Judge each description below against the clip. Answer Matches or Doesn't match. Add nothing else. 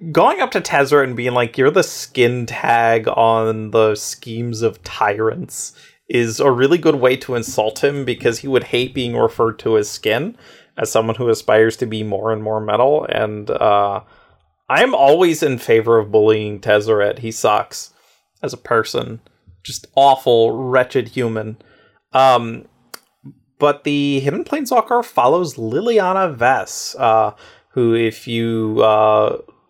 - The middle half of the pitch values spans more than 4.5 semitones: Doesn't match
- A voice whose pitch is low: Matches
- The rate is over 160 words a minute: Doesn't match